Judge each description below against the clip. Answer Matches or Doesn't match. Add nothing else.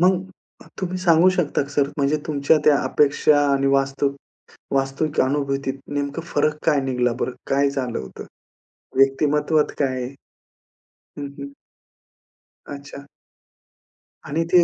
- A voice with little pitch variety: Matches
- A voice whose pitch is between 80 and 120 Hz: Doesn't match